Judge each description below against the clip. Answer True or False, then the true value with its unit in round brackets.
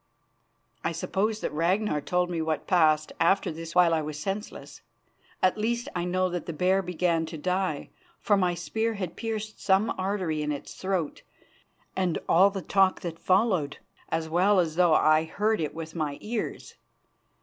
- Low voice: False (180 Hz)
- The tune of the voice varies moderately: True (3.4 semitones)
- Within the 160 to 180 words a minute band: True (170 wpm)